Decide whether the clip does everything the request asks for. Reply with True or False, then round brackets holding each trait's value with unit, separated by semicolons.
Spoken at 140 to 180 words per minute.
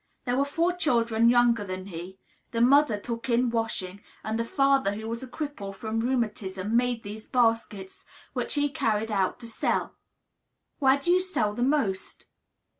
True (170 wpm)